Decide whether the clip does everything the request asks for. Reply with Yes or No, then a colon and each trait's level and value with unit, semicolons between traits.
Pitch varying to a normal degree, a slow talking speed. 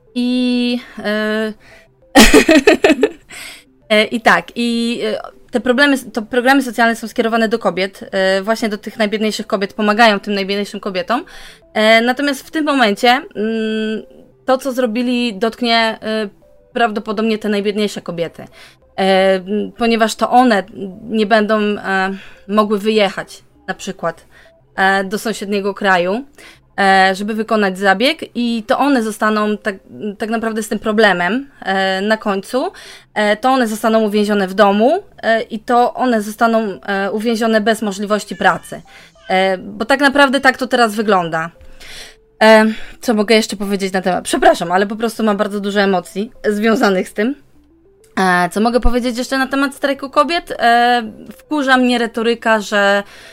No: average, 3.1 semitones; average, 135 wpm